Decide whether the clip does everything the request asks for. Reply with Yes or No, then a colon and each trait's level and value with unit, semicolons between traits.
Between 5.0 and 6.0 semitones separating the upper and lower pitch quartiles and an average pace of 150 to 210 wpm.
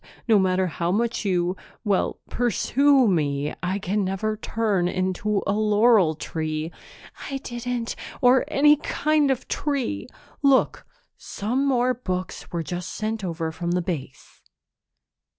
No: wide, 5.6 semitones; slow, 135 wpm